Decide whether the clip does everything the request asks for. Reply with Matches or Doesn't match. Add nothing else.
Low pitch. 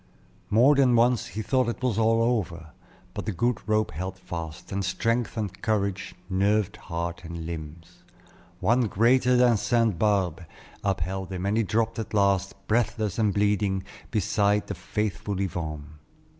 Matches